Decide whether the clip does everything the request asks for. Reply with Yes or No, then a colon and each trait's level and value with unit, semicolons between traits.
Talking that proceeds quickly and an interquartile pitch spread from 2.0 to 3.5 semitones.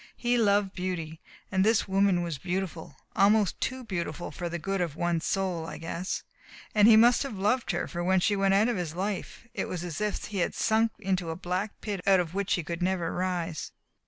Yes: fast, 215 wpm; average, 2.9 semitones